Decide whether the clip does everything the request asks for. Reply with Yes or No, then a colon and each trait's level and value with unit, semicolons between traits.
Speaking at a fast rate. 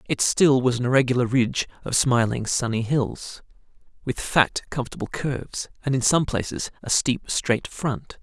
No: average, 160 wpm